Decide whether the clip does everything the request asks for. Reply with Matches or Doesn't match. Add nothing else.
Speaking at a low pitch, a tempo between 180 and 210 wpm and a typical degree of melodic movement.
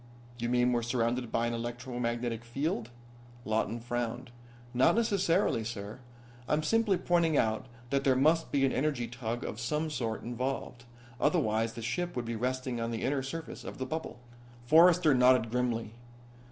Doesn't match